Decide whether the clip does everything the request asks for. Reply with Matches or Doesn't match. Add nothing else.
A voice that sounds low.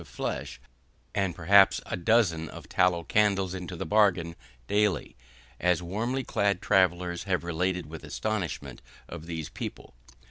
Matches